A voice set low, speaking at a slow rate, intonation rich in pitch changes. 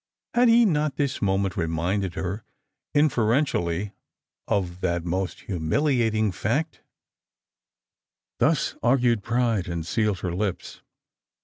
Yes: low, 105 Hz; slow, 105 wpm; wide, 5.8 semitones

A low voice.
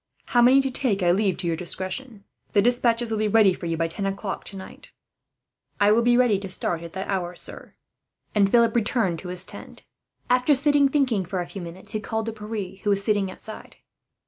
No: high, 205 Hz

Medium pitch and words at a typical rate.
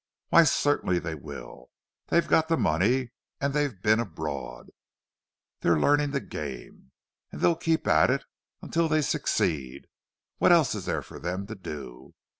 No: low, 100 Hz; average, 145 wpm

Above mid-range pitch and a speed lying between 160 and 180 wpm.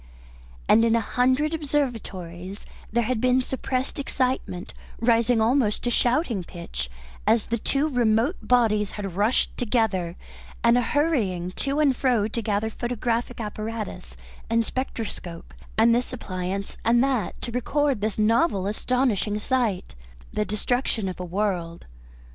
No: high, 230 Hz; slow, 135 wpm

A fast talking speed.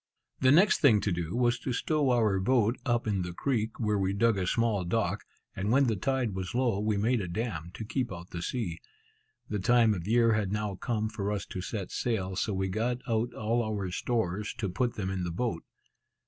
Yes: fast, 220 wpm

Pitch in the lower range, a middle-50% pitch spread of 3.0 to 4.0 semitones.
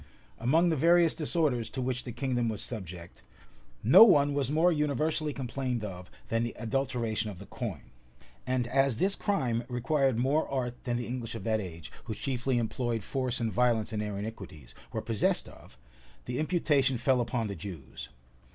Yes: low, 125 Hz; average, 3.7 semitones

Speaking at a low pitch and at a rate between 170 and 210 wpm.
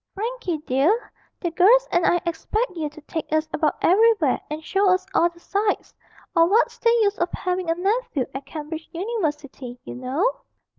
No: very high, 345 Hz; average, 180 wpm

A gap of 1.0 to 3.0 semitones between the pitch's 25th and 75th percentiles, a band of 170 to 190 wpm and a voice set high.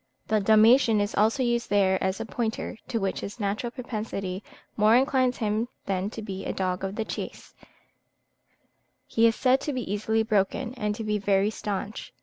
Yes: average, 2.7 semitones; average, 180 wpm; high, 215 Hz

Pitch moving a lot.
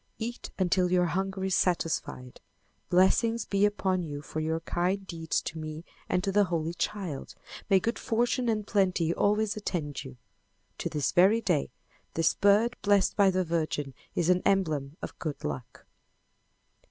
No: average, 4.0 semitones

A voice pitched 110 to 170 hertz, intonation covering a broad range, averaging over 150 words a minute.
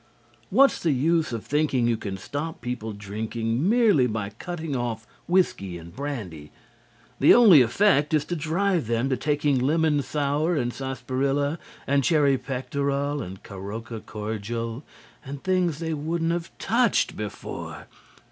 No: medium, 140 Hz; wide, 5.7 semitones; average, 140 wpm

